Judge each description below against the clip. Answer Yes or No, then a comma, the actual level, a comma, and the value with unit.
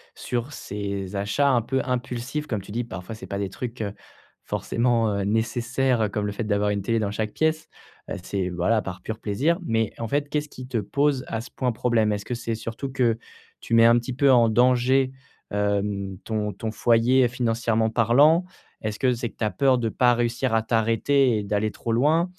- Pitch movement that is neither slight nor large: Yes, average, 3.3 semitones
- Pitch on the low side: Yes, low, 115 Hz